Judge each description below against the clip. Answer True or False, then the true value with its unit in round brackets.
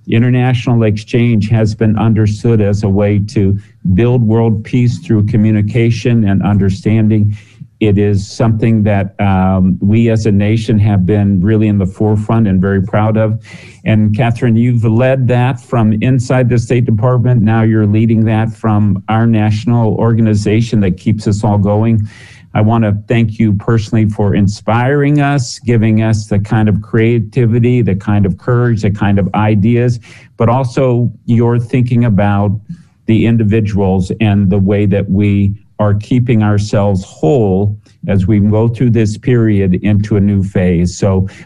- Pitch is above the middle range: False (110 Hz)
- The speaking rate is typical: True (155 wpm)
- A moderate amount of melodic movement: False (2.3 semitones)